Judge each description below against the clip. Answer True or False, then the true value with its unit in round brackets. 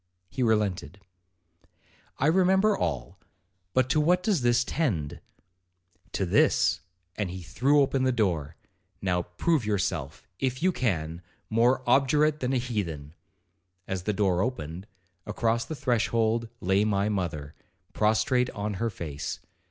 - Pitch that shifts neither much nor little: False (6.2 semitones)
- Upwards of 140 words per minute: False (135 wpm)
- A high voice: False (110 Hz)